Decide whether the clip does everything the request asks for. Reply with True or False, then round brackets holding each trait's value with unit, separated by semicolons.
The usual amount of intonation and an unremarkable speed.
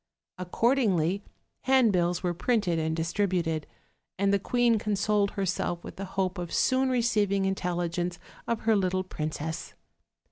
False (3.5 semitones; 130 wpm)